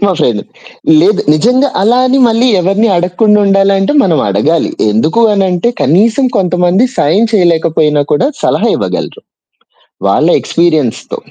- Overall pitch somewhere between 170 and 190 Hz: Yes, medium, 185 Hz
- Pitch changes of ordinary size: Yes, average, 5.0 semitones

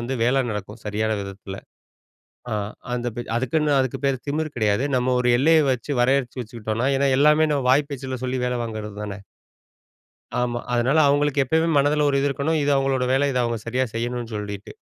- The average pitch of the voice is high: No, low, 125 Hz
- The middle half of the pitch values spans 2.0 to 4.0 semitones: Yes, average, 3.4 semitones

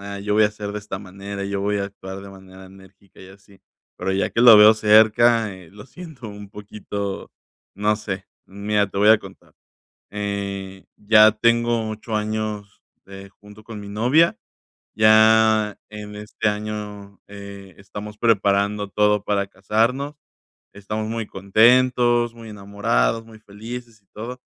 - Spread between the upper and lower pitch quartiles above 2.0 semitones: No, narrow, 1.6 semitones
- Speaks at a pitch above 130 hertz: No, low, 105 Hz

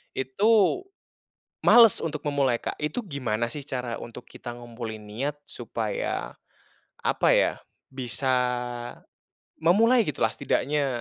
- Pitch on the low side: Yes, low, 130 Hz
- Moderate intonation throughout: Yes, average, 4.5 semitones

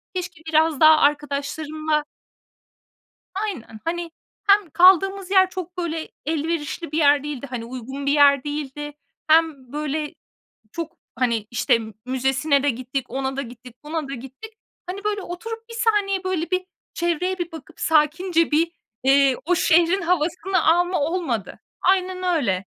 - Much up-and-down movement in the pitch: No, average, 4.4 semitones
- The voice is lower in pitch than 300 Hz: No, very high, 315 Hz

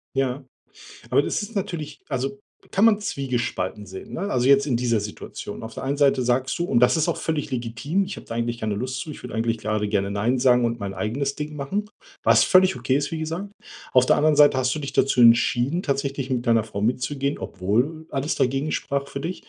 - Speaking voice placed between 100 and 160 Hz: Yes, low, 135 Hz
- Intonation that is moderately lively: Yes, average, 4.1 semitones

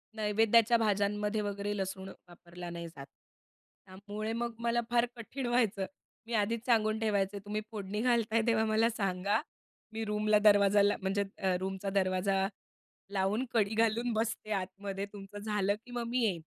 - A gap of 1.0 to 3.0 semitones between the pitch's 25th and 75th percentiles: Yes, narrow, 2.4 semitones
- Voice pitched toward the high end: Yes, high, 210 Hz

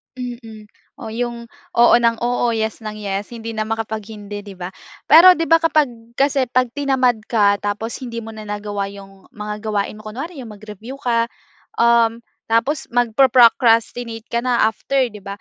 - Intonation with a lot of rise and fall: No, narrow, 2.5 semitones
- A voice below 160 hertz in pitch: No, high, 230 Hz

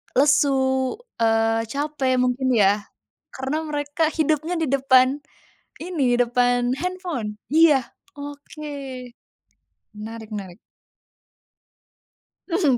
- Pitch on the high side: Yes, very high, 270 Hz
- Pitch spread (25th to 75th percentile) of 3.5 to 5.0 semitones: Yes, average, 4.0 semitones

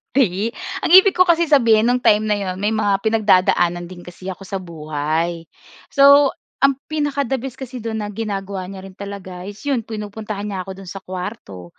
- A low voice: No, high, 205 Hz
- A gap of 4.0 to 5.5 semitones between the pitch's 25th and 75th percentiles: Yes, average, 4.7 semitones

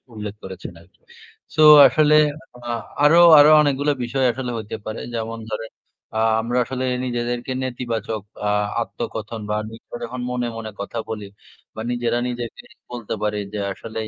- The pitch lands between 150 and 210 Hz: No, low, 120 Hz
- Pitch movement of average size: No, narrow, 2.2 semitones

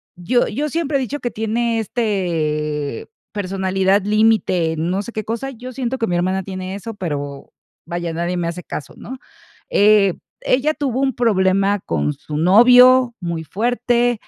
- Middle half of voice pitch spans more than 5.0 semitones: Yes, wide, 5.5 semitones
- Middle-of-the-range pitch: No, high, 205 Hz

